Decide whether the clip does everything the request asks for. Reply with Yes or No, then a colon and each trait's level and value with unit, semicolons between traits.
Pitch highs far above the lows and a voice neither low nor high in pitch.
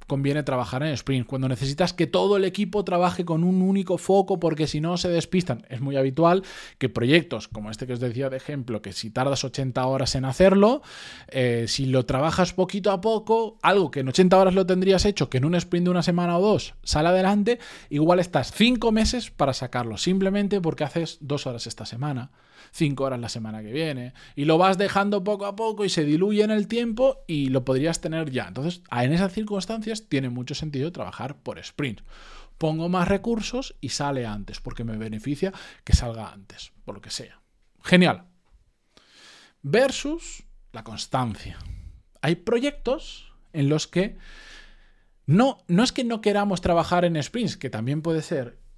Yes: wide, 6.8 semitones; medium, 160 Hz